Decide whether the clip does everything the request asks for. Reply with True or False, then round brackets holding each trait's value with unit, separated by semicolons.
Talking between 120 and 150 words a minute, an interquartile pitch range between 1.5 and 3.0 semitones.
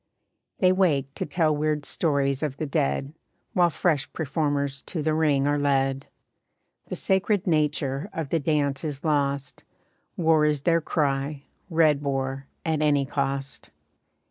True (145 wpm; 2.5 semitones)